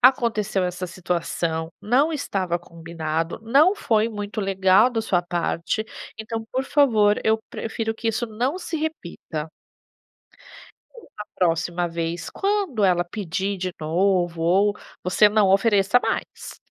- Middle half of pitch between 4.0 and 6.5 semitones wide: Yes, average, 4.5 semitones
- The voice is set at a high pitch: Yes, high, 195 Hz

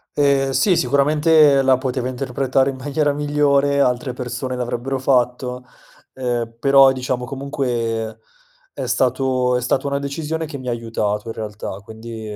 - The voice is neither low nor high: No, low, 130 Hz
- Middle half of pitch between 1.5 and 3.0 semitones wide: Yes, narrow, 2.4 semitones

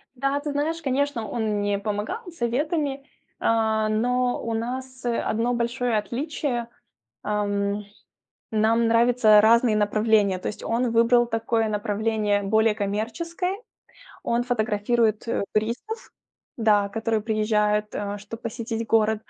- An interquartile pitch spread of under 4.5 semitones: Yes, narrow, 2.5 semitones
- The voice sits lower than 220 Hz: No, high, 225 Hz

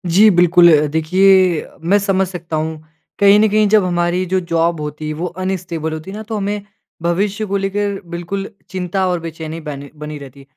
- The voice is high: No, medium, 180 Hz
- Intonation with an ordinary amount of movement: Yes, average, 3.5 semitones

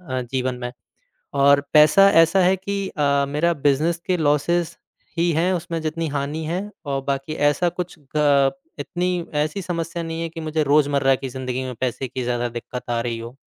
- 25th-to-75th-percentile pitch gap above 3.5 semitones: Yes, average, 4.0 semitones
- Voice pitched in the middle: Yes, medium, 150 Hz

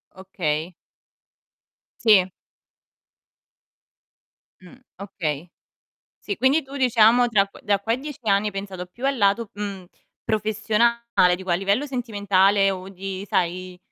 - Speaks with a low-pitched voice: No, high, 200 Hz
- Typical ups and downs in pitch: Yes, average, 3.8 semitones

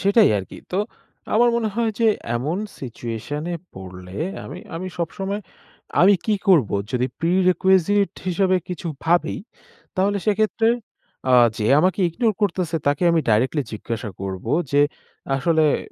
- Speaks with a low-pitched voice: No, medium, 170 Hz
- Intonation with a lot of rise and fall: Yes, wide, 7.7 semitones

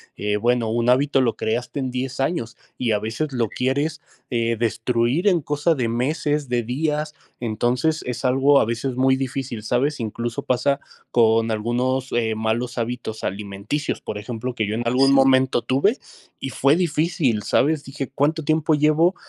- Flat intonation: No, average, 3.7 semitones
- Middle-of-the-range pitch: No, low, 125 Hz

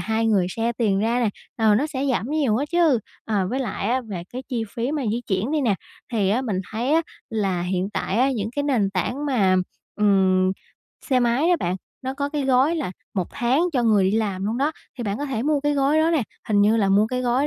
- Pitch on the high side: Yes, high, 235 Hz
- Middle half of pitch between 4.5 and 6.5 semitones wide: Yes, average, 5.0 semitones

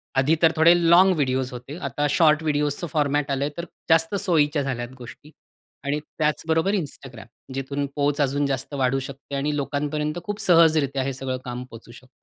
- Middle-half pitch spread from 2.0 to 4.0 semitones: Yes, narrow, 2.6 semitones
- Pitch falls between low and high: Yes, medium, 145 Hz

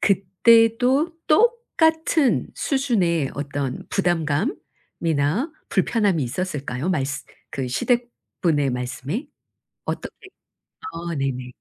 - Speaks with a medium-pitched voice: Yes, medium, 180 Hz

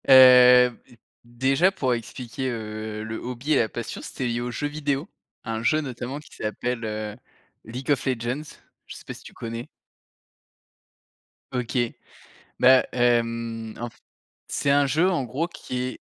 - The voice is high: No, low, 125 Hz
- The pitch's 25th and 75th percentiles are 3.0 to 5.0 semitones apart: No, narrow, 2.6 semitones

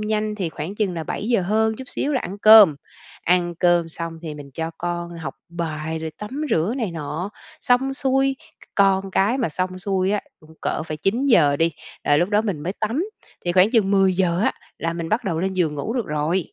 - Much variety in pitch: No, average, 4.5 semitones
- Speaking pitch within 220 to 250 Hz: No, medium, 185 Hz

